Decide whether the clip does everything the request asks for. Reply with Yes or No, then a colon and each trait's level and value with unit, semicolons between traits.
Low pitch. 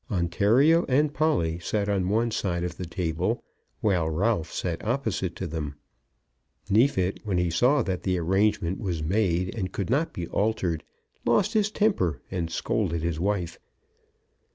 Yes: very low, 95 Hz